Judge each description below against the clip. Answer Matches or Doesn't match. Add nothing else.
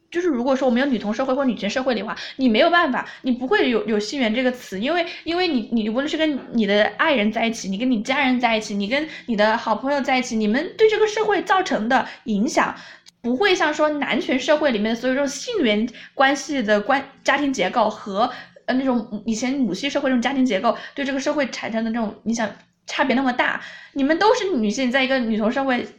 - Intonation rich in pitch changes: Doesn't match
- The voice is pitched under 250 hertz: Doesn't match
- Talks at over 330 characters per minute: Matches